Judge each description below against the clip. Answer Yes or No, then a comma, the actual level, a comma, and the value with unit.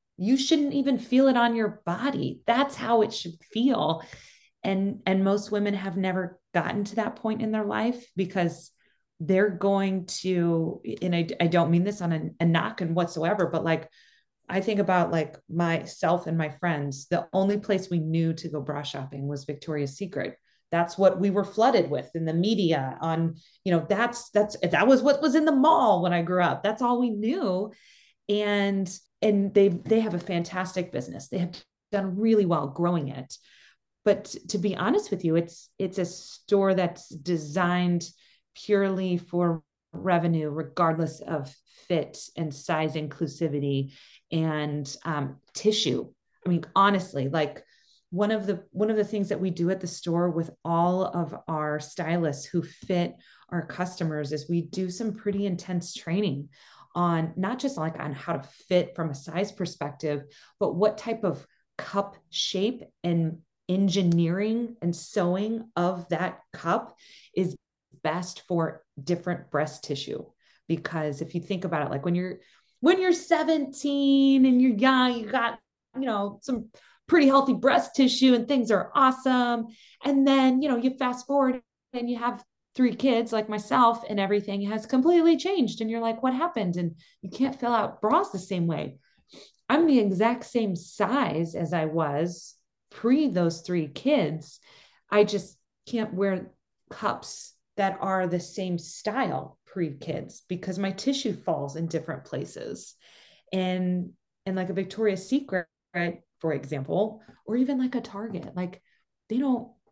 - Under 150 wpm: No, average, 165 wpm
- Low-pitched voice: No, medium, 185 Hz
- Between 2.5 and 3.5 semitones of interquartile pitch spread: No, average, 4.8 semitones